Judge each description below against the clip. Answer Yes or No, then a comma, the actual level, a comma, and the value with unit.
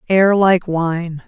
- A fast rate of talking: No, average, 140 wpm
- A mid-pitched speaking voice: Yes, medium, 175 Hz